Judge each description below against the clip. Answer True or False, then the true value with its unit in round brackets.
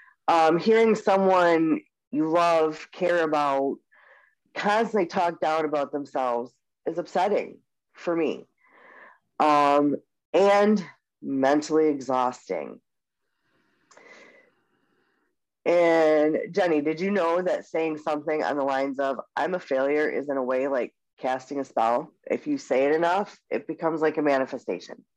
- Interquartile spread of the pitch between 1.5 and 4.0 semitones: False (4.5 semitones)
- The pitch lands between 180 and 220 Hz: False (155 Hz)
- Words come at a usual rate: False (125 wpm)